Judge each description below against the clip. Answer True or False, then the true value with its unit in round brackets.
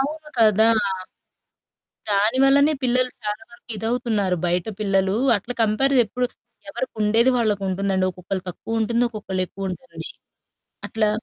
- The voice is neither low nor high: False (215 Hz)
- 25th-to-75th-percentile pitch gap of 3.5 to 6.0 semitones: True (4.0 semitones)